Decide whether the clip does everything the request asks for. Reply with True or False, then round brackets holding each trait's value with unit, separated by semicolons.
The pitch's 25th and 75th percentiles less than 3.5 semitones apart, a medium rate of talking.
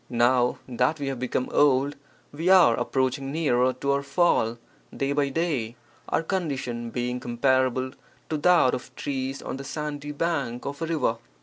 True (2.8 semitones; 170 wpm)